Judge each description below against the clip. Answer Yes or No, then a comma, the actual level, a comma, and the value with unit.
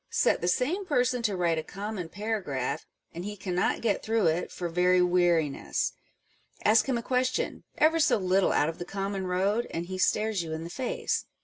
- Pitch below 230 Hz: Yes, high, 190 Hz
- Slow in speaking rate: No, average, 195 wpm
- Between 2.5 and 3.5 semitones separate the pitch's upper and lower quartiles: No, average, 4.3 semitones